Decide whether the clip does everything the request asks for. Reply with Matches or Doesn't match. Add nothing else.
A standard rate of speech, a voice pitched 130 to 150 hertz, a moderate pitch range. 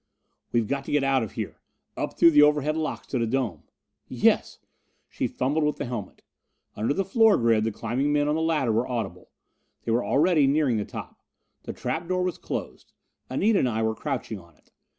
Doesn't match